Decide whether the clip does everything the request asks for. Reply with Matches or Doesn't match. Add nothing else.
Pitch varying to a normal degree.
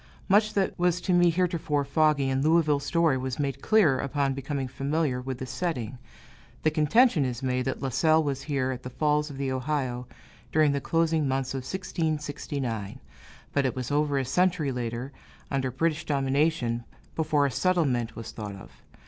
Matches